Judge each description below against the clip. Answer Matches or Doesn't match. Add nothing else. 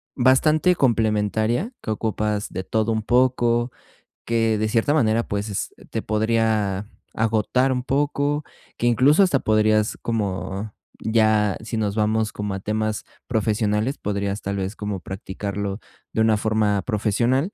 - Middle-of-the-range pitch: Doesn't match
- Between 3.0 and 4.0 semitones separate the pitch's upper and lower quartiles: Doesn't match